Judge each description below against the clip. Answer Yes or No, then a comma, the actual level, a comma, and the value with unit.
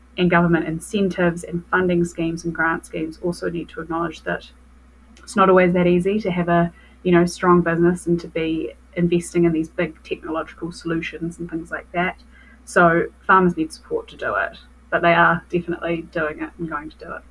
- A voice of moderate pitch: Yes, medium, 170 Hz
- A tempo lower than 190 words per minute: No, average, 200 wpm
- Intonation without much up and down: Yes, narrow, 1.3 semitones